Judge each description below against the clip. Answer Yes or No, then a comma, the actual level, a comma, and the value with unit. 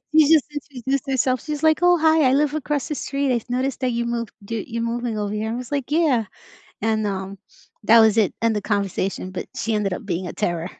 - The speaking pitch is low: No, high, 235 Hz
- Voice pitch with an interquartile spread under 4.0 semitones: No, average, 5.0 semitones